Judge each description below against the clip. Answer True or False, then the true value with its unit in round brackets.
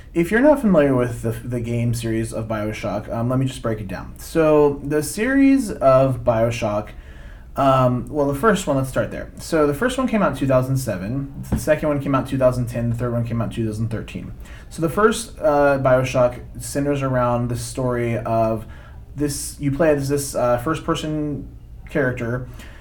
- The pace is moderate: True (190 wpm)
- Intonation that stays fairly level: False (4.0 semitones)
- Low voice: True (130 Hz)